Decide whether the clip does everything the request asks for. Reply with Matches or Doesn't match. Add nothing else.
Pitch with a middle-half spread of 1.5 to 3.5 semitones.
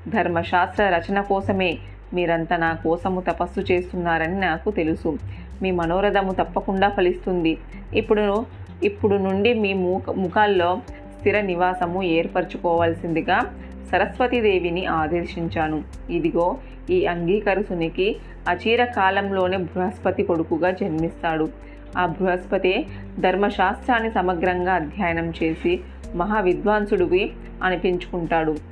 Matches